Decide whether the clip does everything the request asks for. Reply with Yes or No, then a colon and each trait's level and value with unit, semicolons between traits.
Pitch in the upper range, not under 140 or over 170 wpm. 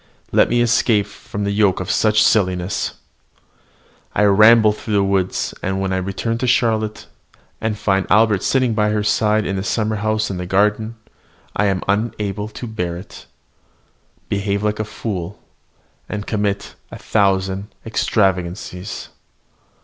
No: low, 105 Hz; average, 150 wpm